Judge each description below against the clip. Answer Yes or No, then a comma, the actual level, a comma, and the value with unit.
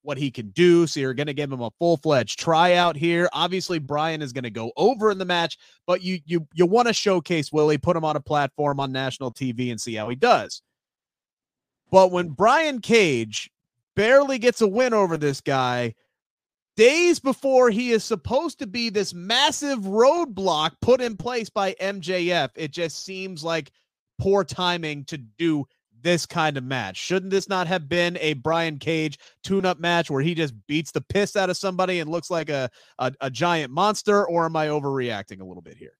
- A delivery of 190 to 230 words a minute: Yes, average, 200 wpm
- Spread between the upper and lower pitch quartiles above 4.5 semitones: Yes, average, 5.0 semitones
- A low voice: No, medium, 170 Hz